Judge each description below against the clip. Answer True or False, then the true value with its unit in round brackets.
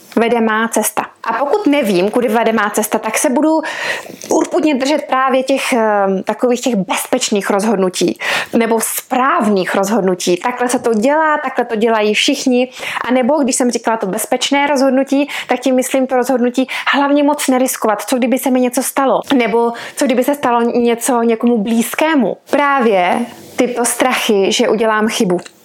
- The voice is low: False (250 Hz)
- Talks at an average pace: True (160 wpm)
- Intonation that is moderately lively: True (3.4 semitones)